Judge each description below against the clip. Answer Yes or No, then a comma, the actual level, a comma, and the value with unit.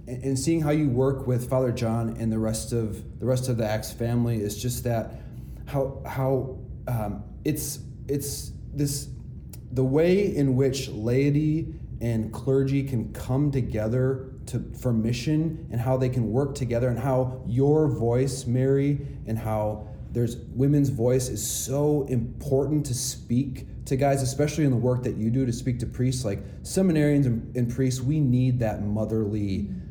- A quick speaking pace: No, average, 165 wpm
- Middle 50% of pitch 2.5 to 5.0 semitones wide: Yes, average, 2.8 semitones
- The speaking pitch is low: Yes, low, 125 Hz